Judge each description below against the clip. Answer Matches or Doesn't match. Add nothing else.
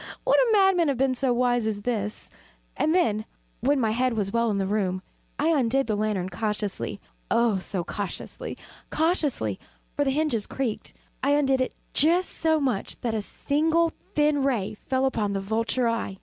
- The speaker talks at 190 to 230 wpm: Doesn't match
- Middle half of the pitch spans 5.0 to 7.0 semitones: Matches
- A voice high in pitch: Matches